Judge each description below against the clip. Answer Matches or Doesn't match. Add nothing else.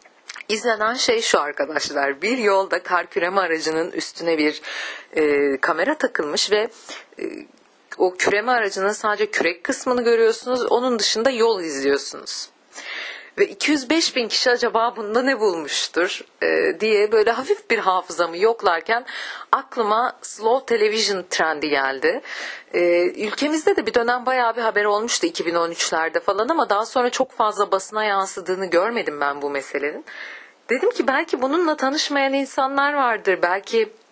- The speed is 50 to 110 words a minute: Doesn't match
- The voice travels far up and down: Matches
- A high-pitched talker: Matches